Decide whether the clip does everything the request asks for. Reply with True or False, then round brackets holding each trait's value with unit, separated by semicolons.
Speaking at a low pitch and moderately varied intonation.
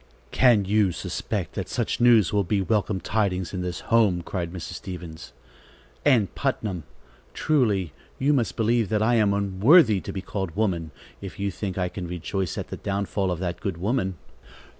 True (100 Hz; 3.3 semitones)